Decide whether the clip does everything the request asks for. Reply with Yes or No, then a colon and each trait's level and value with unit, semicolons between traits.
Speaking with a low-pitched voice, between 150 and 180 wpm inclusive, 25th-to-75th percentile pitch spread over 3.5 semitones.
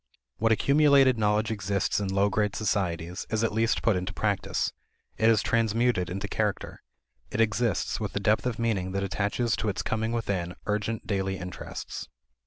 No: low, 105 Hz; average, 170 wpm; average, 2.7 semitones